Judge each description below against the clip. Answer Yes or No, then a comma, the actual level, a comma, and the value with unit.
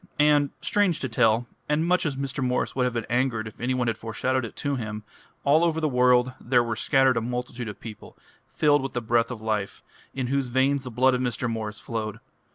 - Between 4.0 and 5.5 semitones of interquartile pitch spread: No, average, 2.9 semitones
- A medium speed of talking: No, fast, 225 wpm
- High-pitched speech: No, low, 125 Hz